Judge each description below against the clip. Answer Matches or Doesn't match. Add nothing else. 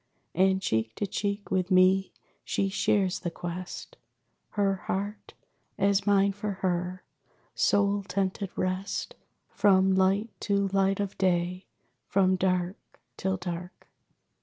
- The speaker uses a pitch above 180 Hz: Matches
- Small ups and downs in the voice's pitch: Matches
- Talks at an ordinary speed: Doesn't match